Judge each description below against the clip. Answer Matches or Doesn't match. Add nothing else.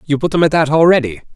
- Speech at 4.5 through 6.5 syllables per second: Doesn't match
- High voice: Doesn't match